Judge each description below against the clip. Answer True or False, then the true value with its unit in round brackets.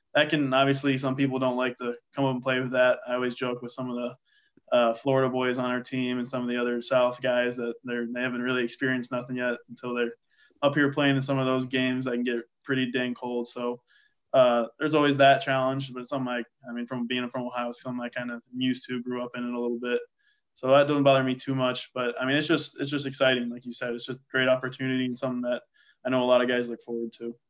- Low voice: True (125 Hz)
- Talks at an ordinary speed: False (270 wpm)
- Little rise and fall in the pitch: True (1.5 semitones)